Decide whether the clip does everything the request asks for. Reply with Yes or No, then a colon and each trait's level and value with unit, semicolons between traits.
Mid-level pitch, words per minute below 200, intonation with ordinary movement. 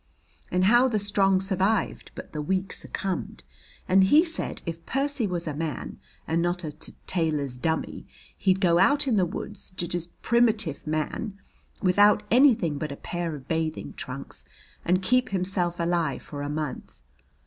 Yes: medium, 180 Hz; average, 165 wpm; average, 4.2 semitones